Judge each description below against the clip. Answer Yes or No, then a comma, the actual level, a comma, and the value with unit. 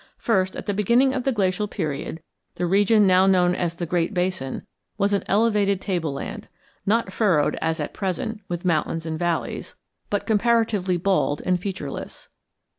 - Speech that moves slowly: No, average, 160 wpm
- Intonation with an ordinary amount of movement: Yes, average, 3.3 semitones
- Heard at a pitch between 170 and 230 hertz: Yes, medium, 185 Hz